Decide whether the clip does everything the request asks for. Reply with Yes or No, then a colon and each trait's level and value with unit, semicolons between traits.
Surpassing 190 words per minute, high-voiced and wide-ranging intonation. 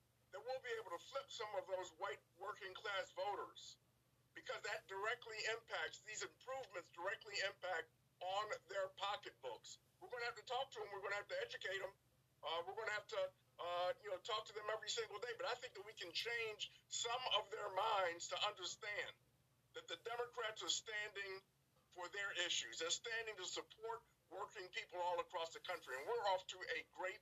Yes: average, 200 wpm; high, 215 Hz; wide, 6.6 semitones